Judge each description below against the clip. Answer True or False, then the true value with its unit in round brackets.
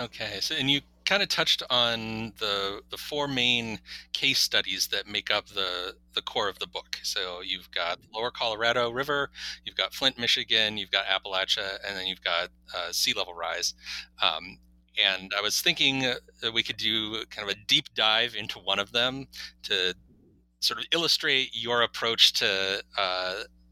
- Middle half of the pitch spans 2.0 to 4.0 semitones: False (5.3 semitones)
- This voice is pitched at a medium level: False (110 Hz)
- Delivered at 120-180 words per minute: True (175 wpm)